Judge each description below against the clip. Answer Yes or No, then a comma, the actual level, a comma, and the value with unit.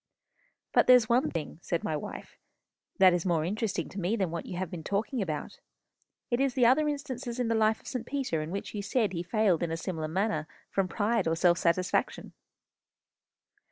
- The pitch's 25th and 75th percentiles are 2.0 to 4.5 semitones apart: No, wide, 5.6 semitones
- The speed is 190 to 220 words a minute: Yes, average, 200 wpm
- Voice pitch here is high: Yes, high, 195 Hz